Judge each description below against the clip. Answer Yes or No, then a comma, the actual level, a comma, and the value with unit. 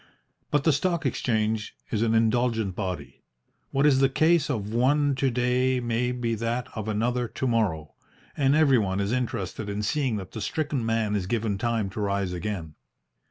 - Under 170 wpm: No, average, 175 wpm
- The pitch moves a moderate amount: Yes, average, 3.8 semitones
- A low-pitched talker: Yes, low, 115 Hz